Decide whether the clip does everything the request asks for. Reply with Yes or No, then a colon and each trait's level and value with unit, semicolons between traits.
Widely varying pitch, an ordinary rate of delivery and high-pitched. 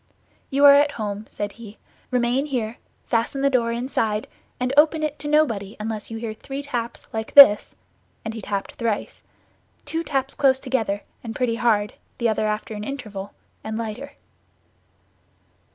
No: average, 4.1 semitones; average, 155 wpm; high, 235 Hz